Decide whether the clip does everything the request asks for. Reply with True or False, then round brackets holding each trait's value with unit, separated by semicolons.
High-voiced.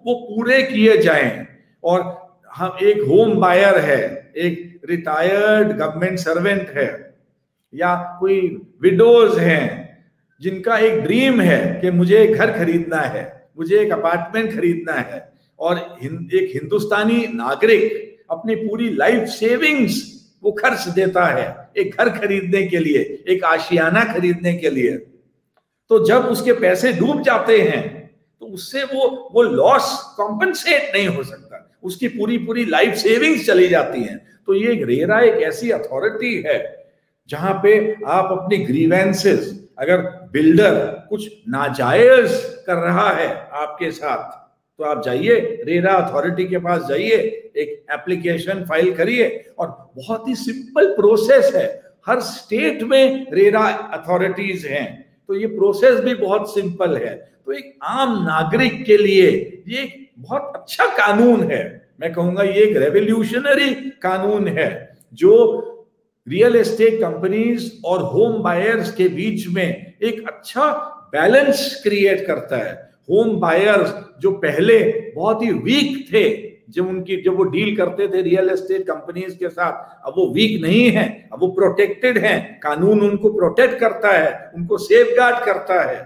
True (210 Hz)